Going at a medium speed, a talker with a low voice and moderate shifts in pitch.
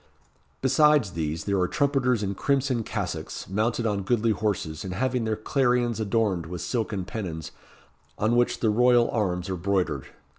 Yes: average, 155 wpm; low, 110 Hz; average, 4.5 semitones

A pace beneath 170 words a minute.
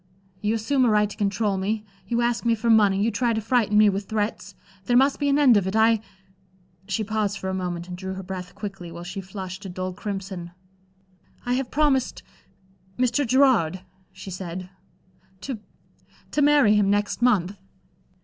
No: average, 185 wpm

